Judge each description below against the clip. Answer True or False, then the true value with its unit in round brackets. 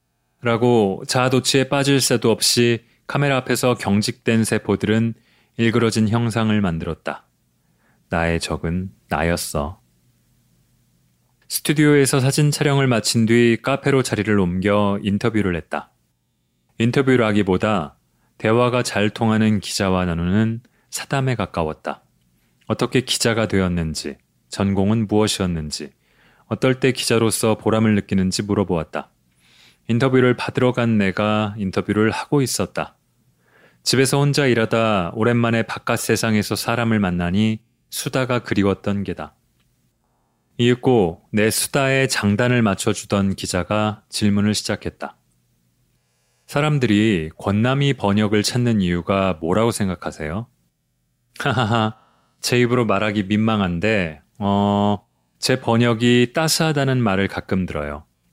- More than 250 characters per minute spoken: True (275 characters per minute)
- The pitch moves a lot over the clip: False (4.1 semitones)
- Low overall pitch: True (110 Hz)